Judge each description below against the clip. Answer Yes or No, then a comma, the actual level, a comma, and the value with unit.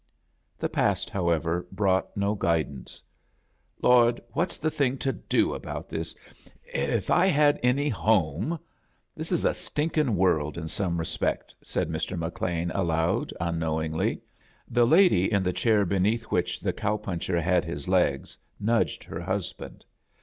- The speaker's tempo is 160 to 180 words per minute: No, average, 145 wpm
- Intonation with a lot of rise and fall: Yes, wide, 6.5 semitones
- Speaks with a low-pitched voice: Yes, very low, 95 Hz